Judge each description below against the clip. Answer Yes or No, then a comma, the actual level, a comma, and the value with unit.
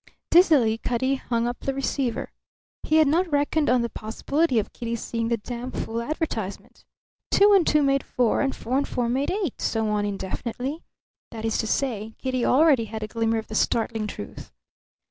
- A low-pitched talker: No, high, 245 Hz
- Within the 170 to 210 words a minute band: Yes, average, 185 wpm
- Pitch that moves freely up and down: No, average, 4.0 semitones